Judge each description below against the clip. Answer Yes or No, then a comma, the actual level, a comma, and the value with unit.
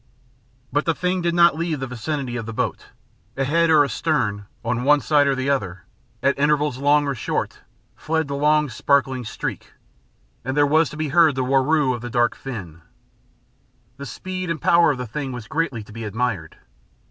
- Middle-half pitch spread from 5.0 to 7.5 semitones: No, average, 3.9 semitones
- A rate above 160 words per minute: Yes, average, 195 wpm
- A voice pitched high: No, medium, 140 Hz